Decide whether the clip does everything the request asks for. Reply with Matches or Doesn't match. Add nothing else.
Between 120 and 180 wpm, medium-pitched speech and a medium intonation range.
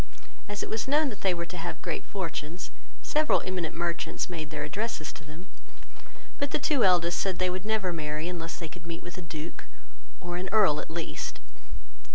Doesn't match